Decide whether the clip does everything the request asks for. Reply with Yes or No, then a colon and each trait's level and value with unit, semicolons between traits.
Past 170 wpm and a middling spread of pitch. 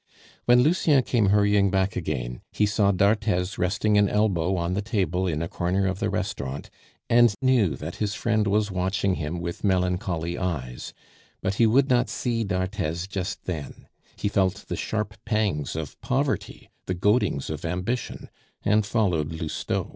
No: average, 160 wpm; average, 3.4 semitones